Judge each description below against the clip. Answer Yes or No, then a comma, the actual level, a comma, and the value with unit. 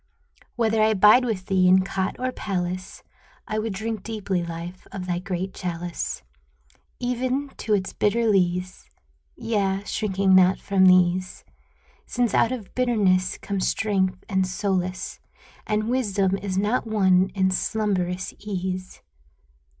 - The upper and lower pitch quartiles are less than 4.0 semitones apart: Yes, average, 2.8 semitones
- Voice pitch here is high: Yes, high, 195 Hz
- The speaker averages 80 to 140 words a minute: Yes, slow, 135 wpm